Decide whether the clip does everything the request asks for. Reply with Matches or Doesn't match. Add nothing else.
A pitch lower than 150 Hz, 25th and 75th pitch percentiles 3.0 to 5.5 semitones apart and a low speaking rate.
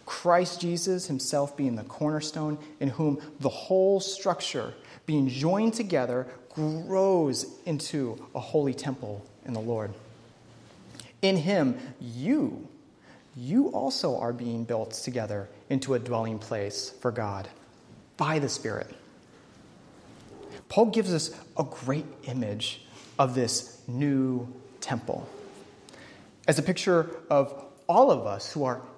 Matches